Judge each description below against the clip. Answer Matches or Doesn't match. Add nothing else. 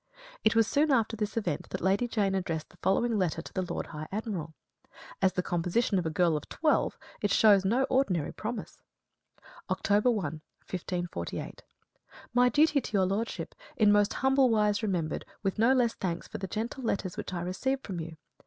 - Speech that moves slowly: Doesn't match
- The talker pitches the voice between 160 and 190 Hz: Doesn't match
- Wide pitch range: Doesn't match